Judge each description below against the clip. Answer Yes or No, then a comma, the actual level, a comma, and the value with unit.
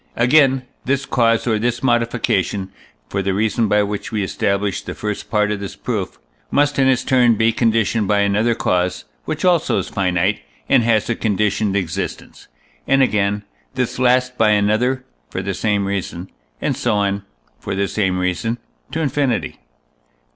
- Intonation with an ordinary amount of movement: Yes, average, 3.5 semitones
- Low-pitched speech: Yes, low, 105 Hz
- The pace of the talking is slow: No, average, 165 wpm